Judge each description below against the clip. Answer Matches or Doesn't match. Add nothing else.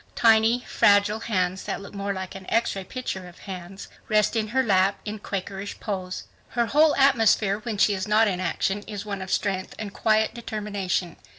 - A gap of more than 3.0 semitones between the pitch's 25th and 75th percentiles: Doesn't match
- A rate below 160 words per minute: Doesn't match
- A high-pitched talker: Matches